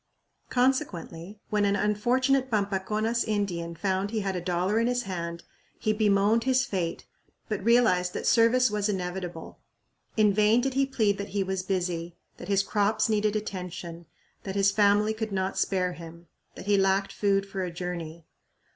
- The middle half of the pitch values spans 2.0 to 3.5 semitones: Yes, average, 3.0 semitones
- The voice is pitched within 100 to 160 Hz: No, high, 200 Hz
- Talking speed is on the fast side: No, average, 165 wpm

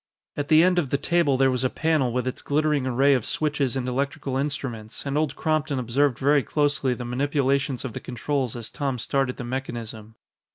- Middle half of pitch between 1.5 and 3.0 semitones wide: Yes, narrow, 2.5 semitones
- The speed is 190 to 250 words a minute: Yes, average, 200 wpm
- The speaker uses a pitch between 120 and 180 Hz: Yes, low, 135 Hz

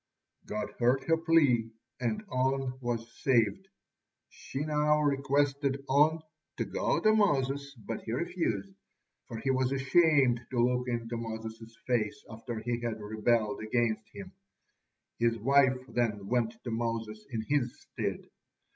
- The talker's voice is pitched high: No, low, 125 Hz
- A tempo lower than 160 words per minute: Yes, average, 140 wpm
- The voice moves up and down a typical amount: Yes, average, 3.4 semitones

